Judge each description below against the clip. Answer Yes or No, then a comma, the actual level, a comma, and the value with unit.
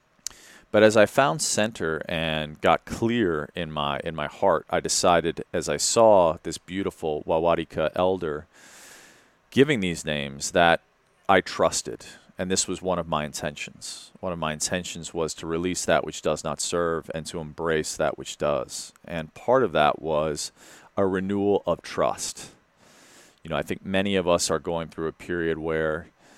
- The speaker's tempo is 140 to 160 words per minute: No, average, 170 wpm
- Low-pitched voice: Yes, very low, 85 Hz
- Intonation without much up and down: No, average, 3.0 semitones